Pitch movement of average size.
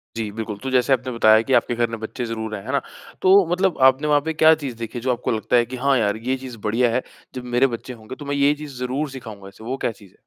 Yes: average, 3.3 semitones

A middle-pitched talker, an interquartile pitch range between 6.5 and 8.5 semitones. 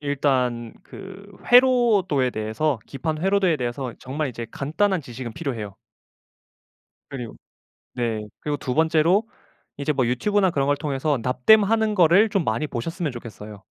Yes: medium, 145 Hz; wide, 7.1 semitones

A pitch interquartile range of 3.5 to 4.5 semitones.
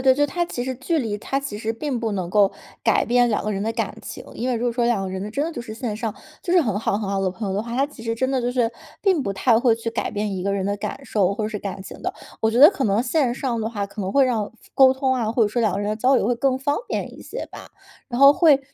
Yes: average, 4.0 semitones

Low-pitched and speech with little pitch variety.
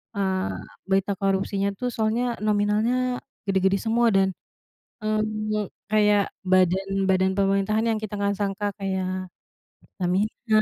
No: high, 200 Hz; narrow, 2.0 semitones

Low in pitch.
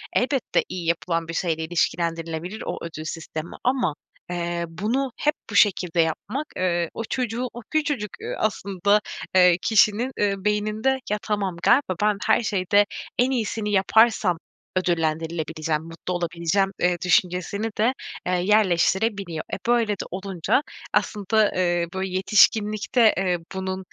No: high, 190 Hz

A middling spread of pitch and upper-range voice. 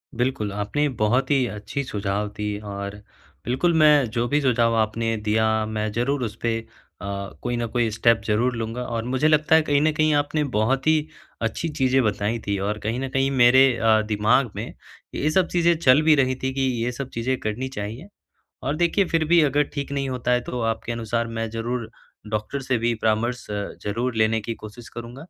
No: average, 3.9 semitones; low, 120 Hz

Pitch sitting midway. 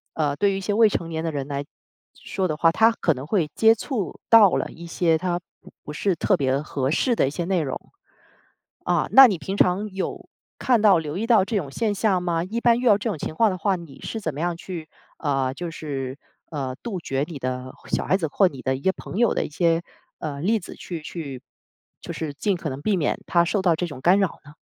Yes: medium, 170 Hz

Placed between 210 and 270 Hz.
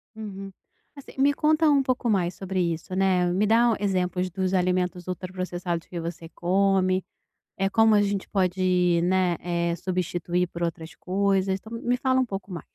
No: medium, 185 Hz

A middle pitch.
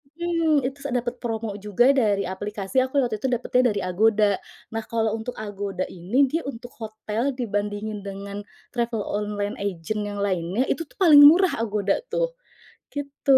No: high, 220 Hz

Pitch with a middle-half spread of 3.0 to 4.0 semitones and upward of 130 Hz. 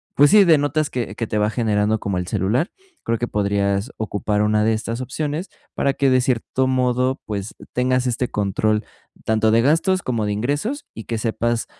No: average, 3.7 semitones; low, 115 Hz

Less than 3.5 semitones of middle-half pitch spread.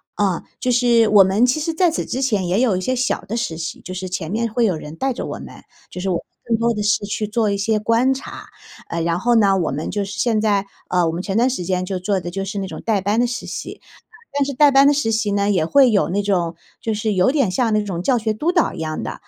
No: average, 4.3 semitones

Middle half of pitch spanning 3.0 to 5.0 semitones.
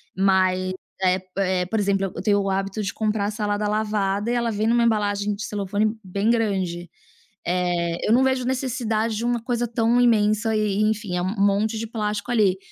No: narrow, 2.5 semitones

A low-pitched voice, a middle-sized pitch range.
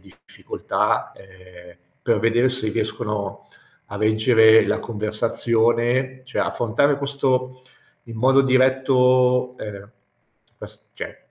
Yes: low, 120 Hz; average, 3.1 semitones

